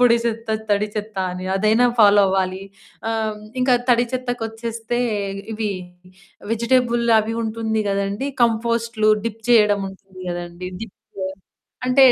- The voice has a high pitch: Yes, high, 220 Hz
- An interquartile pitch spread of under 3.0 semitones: Yes, narrow, 2.4 semitones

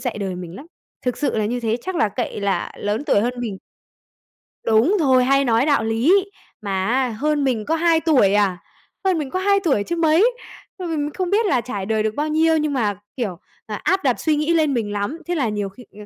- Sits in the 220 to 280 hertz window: Yes, very high, 255 Hz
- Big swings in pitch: Yes, wide, 6.8 semitones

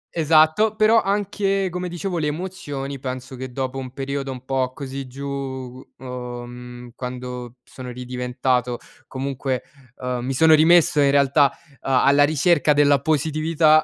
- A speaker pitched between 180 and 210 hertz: No, low, 135 Hz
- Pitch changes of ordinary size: Yes, average, 3.6 semitones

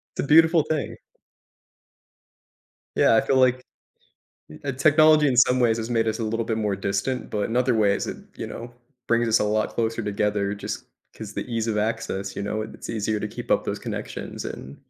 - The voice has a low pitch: Yes, low, 115 Hz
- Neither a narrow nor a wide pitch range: Yes, average, 3.2 semitones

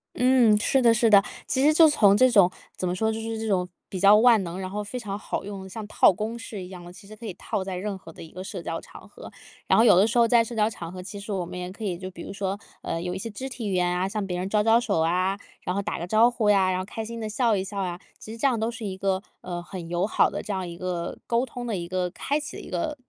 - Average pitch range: Yes, average, 3.6 semitones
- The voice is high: Yes, high, 200 Hz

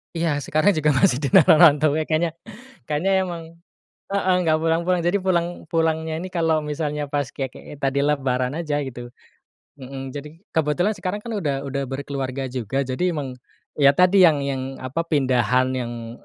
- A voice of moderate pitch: Yes, medium, 150 Hz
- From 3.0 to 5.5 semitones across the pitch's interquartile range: Yes, average, 3.8 semitones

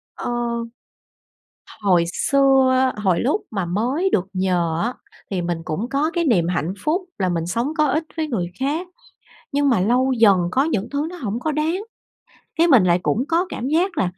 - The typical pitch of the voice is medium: No, high, 245 Hz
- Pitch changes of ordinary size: No, wide, 8.1 semitones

